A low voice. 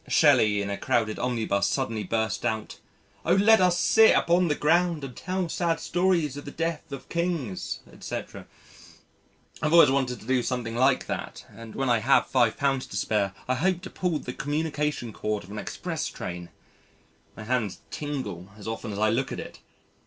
Yes: low, 130 Hz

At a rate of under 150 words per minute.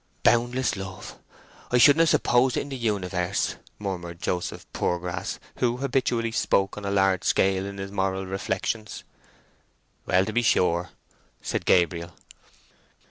Yes: slow, 135 wpm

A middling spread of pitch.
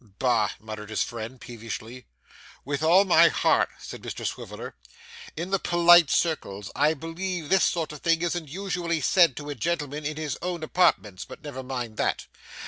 No: wide, 5.8 semitones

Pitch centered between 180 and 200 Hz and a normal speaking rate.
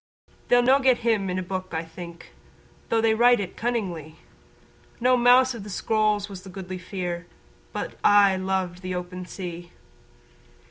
Yes: high, 190 Hz; average, 170 wpm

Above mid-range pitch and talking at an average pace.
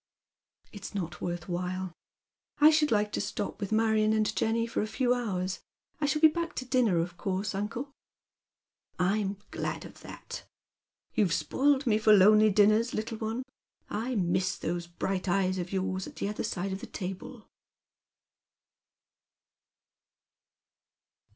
Yes: high, 210 Hz; average, 150 wpm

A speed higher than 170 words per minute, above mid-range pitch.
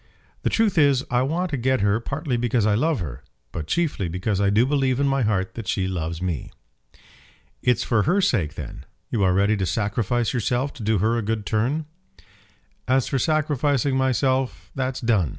No: average, 190 wpm; low, 120 Hz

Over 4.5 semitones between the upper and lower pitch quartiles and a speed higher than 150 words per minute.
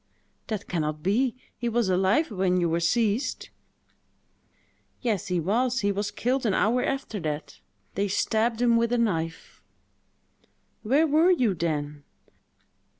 No: average, 5.1 semitones; average, 145 wpm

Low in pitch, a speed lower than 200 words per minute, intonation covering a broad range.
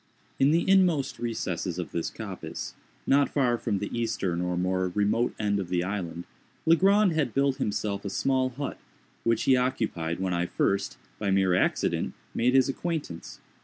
Yes: low, 110 Hz; average, 165 wpm; wide, 6.5 semitones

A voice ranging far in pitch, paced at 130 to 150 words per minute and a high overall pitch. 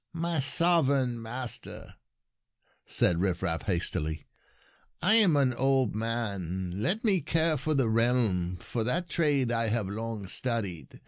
No: wide, 6.4 semitones; average, 140 wpm; low, 120 Hz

